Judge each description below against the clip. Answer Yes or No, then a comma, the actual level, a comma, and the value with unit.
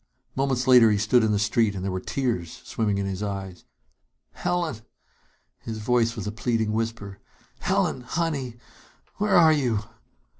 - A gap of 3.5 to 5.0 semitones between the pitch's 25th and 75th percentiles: Yes, average, 4.1 semitones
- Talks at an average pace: Yes, average, 155 wpm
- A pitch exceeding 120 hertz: No, low, 115 Hz